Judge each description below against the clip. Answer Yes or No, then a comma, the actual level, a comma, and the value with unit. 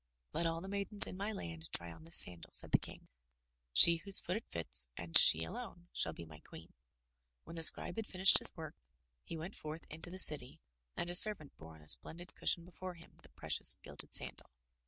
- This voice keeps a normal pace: No, fast, 215 wpm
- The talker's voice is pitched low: No, medium, 165 Hz